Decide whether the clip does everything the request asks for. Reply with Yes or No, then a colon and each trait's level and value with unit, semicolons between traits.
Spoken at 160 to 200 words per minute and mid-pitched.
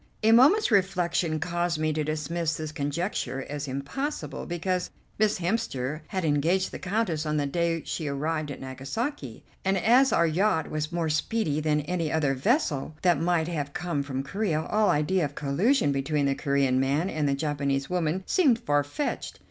Yes: average, 175 wpm; medium, 160 Hz